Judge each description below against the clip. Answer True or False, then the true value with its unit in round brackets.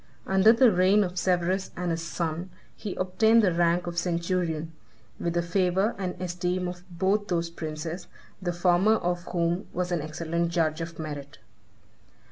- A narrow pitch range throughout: True (1.7 semitones)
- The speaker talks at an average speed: True (160 wpm)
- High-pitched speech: False (175 Hz)